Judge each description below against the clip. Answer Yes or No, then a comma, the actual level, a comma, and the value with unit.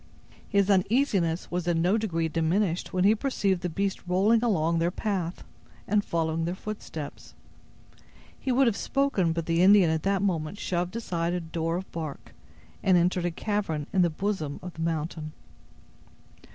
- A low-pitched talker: No, medium, 180 Hz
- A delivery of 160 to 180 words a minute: Yes, average, 165 wpm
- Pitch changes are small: No, average, 3.4 semitones